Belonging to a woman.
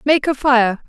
Yes: female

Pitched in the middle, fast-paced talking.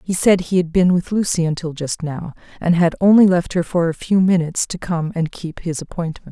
Yes: medium, 175 Hz; fast, 240 wpm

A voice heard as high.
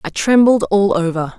Yes: high, 215 Hz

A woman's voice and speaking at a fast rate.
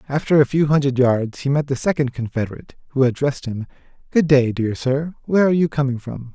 No: male; fast, 210 wpm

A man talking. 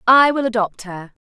No: female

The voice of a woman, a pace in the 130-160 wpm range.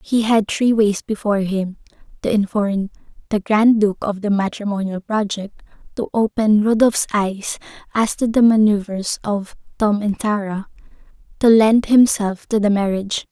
Yes: female; average, 145 wpm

